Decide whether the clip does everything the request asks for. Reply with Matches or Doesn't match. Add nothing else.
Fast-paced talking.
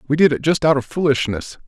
Matches